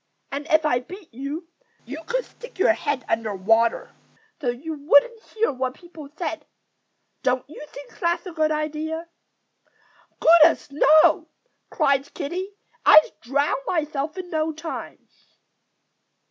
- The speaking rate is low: Yes, slow, 130 wpm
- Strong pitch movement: No, average, 3.3 semitones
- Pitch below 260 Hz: No, very high, 305 Hz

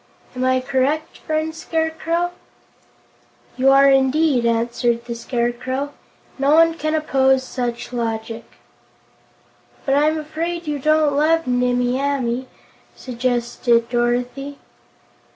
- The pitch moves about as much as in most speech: Yes, average, 4.1 semitones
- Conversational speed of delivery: No, slow, 105 wpm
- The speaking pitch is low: No, very high, 265 Hz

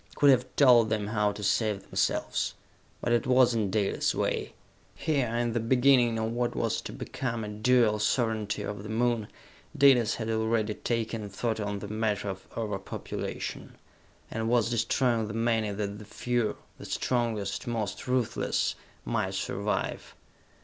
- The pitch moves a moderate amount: No, narrow, 2.3 semitones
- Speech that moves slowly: No, average, 155 wpm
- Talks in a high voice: No, low, 115 Hz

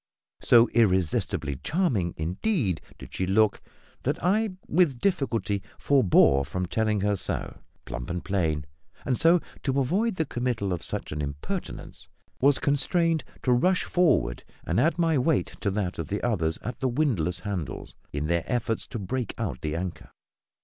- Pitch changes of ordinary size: No, wide, 8.2 semitones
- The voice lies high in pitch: No, low, 110 Hz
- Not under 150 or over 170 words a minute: Yes, average, 160 wpm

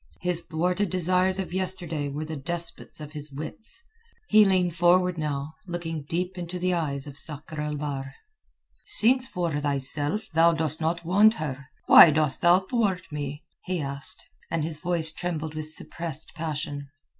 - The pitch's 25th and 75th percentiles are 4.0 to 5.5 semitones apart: No, average, 3.2 semitones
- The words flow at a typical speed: Yes, average, 160 wpm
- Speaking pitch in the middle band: Yes, medium, 165 Hz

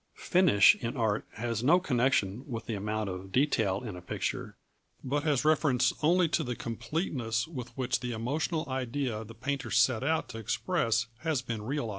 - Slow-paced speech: No, average, 175 wpm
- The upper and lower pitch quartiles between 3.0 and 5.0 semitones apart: Yes, average, 4.3 semitones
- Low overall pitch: Yes, low, 125 Hz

